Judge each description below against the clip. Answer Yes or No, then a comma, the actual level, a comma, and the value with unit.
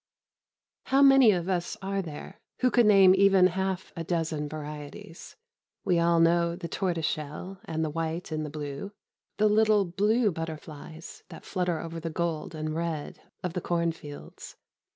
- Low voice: No, medium, 170 Hz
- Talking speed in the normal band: Yes, average, 155 wpm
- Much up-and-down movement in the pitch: No, average, 3.2 semitones